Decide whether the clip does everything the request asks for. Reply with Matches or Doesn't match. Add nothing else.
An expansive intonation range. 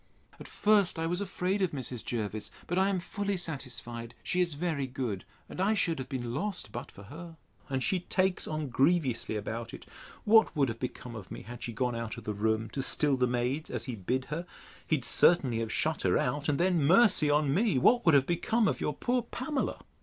Matches